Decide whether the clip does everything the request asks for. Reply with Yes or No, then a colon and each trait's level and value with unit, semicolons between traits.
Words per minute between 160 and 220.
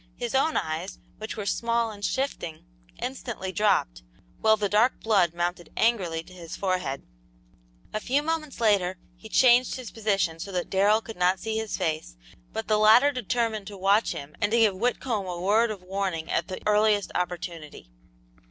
Yes: average, 175 wpm